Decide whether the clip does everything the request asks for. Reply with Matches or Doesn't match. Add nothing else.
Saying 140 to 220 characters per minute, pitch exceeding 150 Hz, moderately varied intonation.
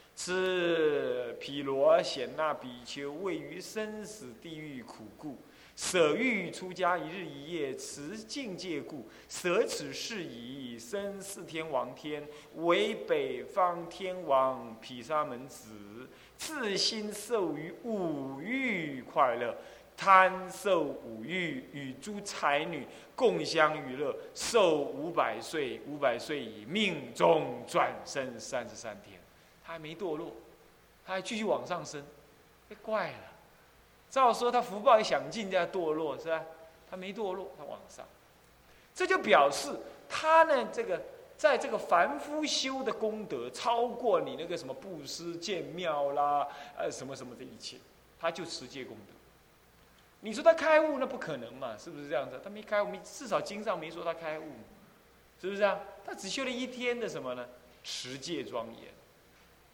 Doesn't match